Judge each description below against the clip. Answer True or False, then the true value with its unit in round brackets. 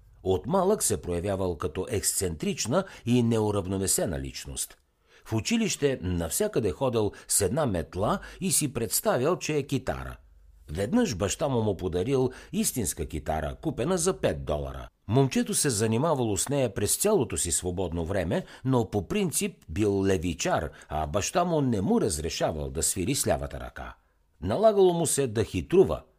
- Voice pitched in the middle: False (105 Hz)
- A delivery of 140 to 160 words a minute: True (145 wpm)